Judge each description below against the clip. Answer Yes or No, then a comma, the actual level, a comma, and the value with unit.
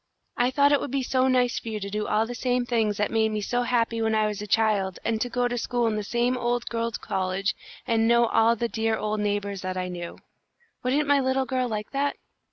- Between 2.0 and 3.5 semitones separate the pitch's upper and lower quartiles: Yes, average, 2.7 semitones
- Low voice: No, high, 230 Hz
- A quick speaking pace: Yes, fast, 245 wpm